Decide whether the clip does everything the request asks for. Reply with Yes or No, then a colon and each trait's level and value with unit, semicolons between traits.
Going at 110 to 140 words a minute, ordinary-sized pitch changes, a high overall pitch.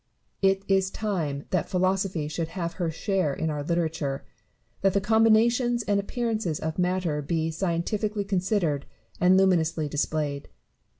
No: slow, 135 wpm; average, 3.8 semitones; medium, 180 Hz